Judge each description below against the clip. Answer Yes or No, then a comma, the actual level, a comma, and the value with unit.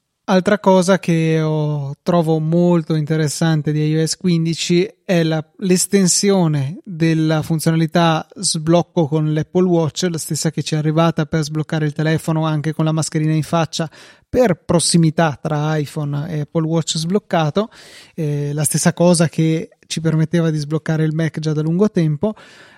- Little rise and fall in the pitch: Yes, narrow, 1.8 semitones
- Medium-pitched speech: Yes, medium, 160 Hz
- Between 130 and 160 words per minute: Yes, average, 150 wpm